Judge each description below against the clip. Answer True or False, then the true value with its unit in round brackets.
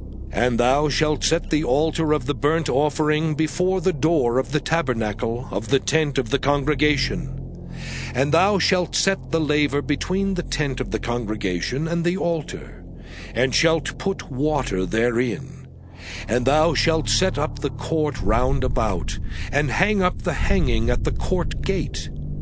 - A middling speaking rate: True (160 wpm)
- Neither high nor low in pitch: True (145 Hz)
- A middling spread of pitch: True (5.0 semitones)